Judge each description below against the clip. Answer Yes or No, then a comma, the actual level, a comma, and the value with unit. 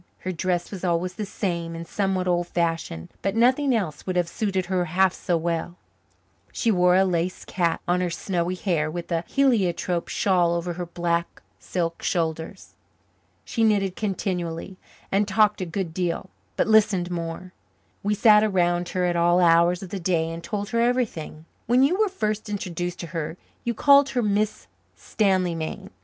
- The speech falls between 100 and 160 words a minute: No, average, 175 wpm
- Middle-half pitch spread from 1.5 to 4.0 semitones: Yes, average, 3.2 semitones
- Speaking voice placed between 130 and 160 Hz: No, medium, 180 Hz